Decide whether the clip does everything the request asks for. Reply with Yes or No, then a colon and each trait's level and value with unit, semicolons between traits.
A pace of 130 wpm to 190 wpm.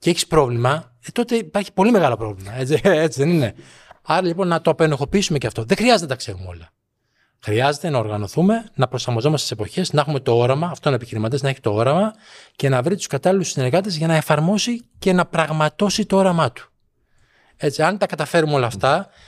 No: fast, 200 wpm